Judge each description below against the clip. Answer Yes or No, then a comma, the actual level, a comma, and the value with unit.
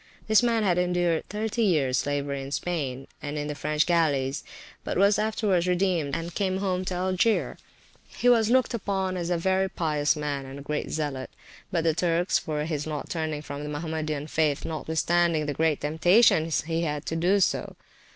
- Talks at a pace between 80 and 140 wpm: No, average, 185 wpm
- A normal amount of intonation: Yes, average, 3.9 semitones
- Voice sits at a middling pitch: Yes, medium, 165 Hz